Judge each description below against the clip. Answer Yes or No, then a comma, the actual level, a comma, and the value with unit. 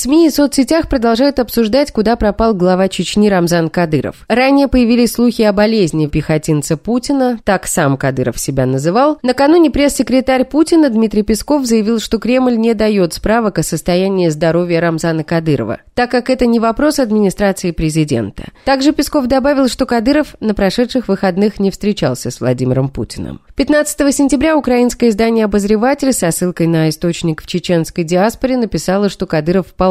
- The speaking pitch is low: No, high, 215 Hz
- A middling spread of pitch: No, wide, 7.2 semitones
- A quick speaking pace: No, average, 150 wpm